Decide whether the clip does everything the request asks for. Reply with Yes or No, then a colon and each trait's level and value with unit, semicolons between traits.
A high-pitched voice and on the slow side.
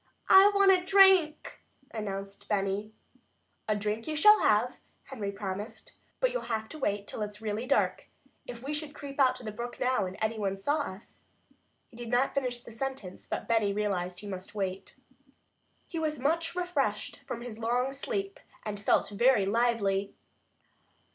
No: high, 230 Hz; average, 175 wpm